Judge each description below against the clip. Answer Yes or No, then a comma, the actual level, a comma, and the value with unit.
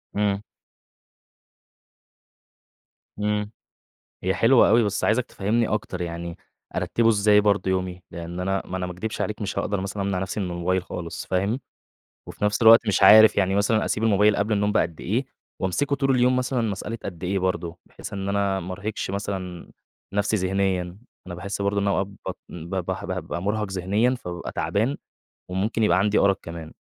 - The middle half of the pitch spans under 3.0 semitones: Yes, narrow, 2.5 semitones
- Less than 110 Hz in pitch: Yes, low, 100 Hz